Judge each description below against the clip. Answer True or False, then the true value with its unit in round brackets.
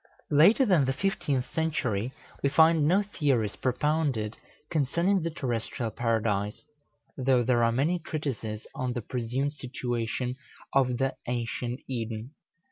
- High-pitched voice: False (130 Hz)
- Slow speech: True (125 wpm)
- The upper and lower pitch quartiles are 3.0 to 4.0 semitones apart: False (4.4 semitones)